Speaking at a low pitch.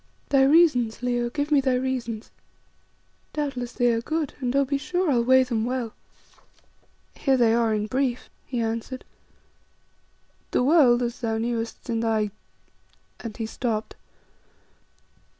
No: high, 245 Hz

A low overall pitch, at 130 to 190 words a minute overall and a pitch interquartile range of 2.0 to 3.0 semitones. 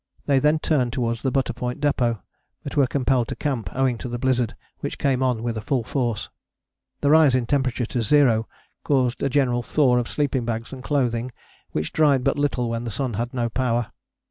No: low, 125 Hz; average, 200 wpm; narrow, 2.6 semitones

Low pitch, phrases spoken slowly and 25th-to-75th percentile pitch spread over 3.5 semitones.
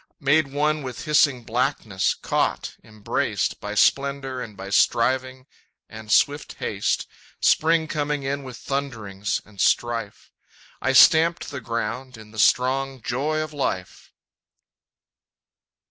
Yes: low, 130 Hz; slow, 120 wpm; average, 4.1 semitones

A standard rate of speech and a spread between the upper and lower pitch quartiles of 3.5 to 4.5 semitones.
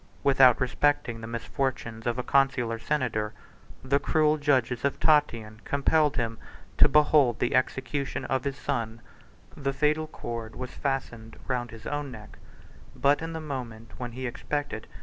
Yes: average, 150 wpm; average, 3.8 semitones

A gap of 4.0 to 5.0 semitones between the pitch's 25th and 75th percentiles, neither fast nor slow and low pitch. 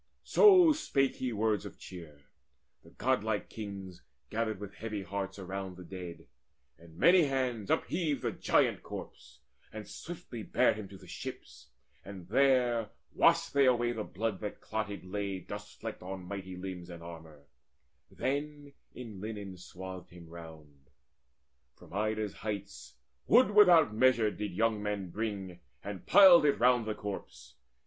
Yes: average, 4.7 semitones; average, 150 wpm; low, 105 Hz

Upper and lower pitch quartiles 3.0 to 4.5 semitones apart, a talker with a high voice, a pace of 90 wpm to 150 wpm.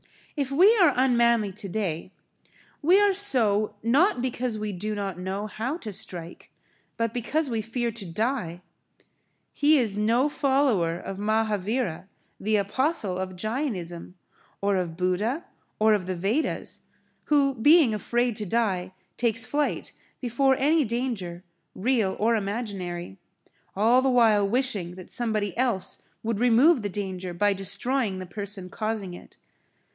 No: average, 4.9 semitones; high, 220 Hz; average, 140 wpm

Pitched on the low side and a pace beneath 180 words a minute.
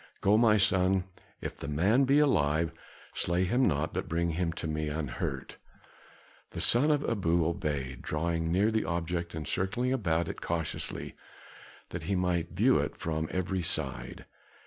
Yes: very low, 85 Hz; average, 160 wpm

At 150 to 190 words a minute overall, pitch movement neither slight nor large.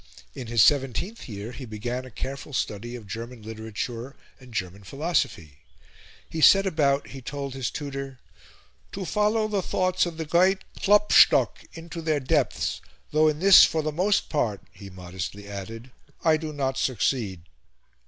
No: average, 155 wpm; wide, 6.3 semitones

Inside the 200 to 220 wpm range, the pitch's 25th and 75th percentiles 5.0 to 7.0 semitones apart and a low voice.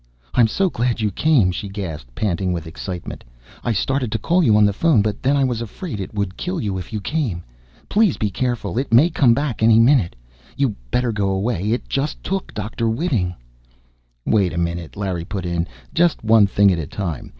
Yes: fast, 205 wpm; wide, 5.4 semitones; low, 110 Hz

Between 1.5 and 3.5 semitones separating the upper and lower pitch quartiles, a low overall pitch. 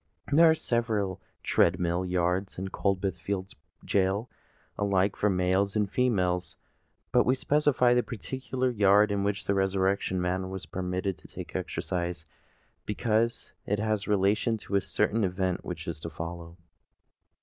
Yes: average, 2.7 semitones; very low, 95 Hz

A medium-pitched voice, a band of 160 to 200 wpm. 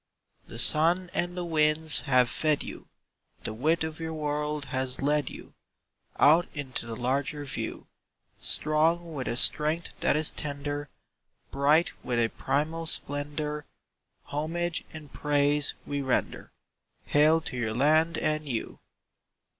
No: medium, 150 Hz; slow, 135 wpm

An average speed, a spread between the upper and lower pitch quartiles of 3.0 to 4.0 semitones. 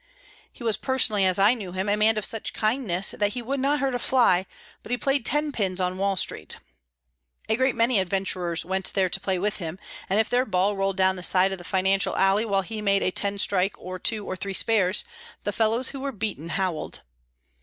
No: fast, 225 wpm; average, 3.3 semitones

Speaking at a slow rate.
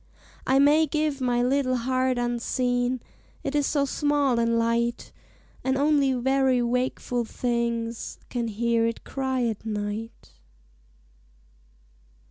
Yes: slow, 115 wpm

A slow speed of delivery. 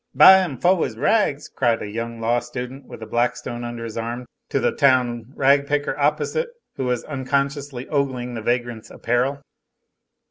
No: average, 170 wpm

